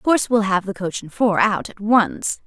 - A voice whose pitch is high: Yes, high, 205 Hz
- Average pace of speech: No, fast, 265 wpm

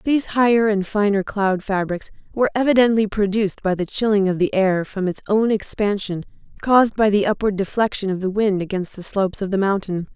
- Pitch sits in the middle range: No, high, 205 Hz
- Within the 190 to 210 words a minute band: Yes, average, 195 wpm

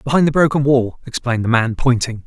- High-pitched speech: No, low, 130 Hz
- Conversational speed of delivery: No, fast, 210 wpm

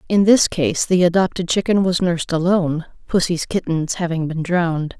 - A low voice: No, medium, 175 Hz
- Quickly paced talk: No, average, 170 wpm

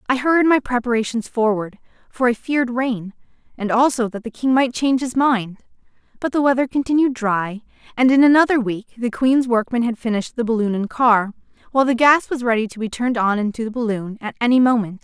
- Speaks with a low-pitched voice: No, high, 240 Hz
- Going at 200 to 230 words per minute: Yes, fast, 205 wpm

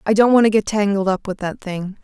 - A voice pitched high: Yes, high, 200 Hz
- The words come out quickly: Yes, fast, 295 wpm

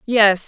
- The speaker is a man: No, female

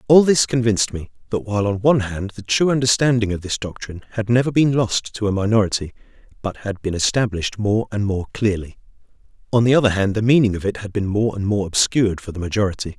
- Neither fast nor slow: No, fast, 215 wpm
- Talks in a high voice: No, low, 105 Hz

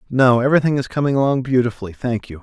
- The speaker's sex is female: No, male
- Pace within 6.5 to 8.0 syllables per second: Yes, 7.2 syllables/s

